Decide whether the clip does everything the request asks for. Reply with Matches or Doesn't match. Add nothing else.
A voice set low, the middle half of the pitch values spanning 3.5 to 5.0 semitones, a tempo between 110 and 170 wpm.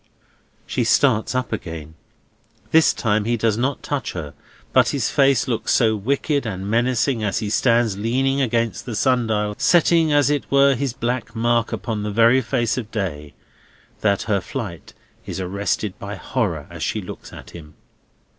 Matches